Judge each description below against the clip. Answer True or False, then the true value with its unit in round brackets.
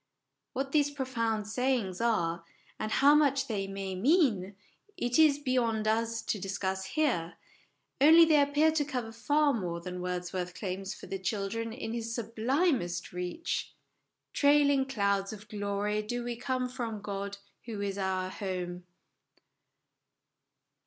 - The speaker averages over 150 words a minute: False (140 wpm)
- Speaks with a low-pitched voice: False (225 Hz)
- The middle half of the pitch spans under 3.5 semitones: False (5.6 semitones)